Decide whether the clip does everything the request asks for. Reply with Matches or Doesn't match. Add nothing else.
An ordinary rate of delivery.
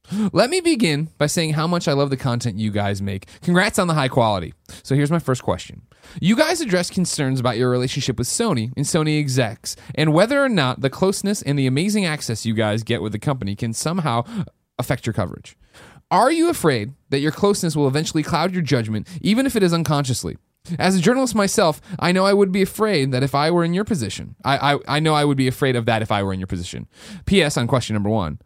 Doesn't match